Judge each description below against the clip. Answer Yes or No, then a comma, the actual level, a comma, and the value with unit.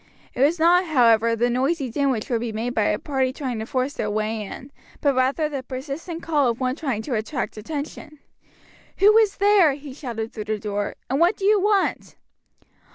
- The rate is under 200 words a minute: No, fast, 205 wpm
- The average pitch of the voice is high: Yes, very high, 265 Hz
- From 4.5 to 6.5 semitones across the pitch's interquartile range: Yes, average, 5.3 semitones